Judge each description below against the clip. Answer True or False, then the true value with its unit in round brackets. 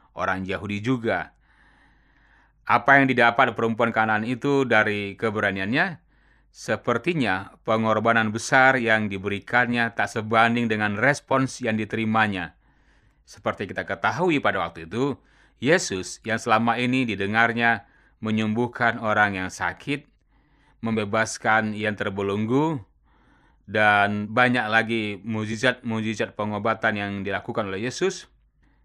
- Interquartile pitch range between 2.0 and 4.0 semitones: True (2.4 semitones)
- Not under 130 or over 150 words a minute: False (100 wpm)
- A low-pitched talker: True (110 Hz)